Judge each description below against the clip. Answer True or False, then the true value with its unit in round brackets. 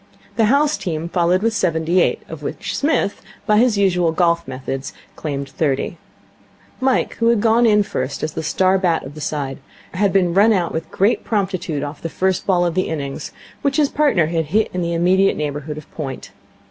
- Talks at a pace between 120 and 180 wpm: False (200 wpm)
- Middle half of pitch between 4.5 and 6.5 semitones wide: True (4.8 semitones)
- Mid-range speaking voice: True (175 Hz)